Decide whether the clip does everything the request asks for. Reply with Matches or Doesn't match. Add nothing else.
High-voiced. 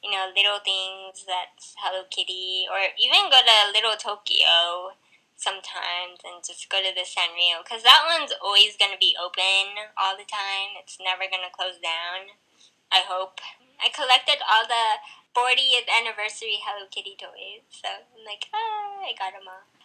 Matches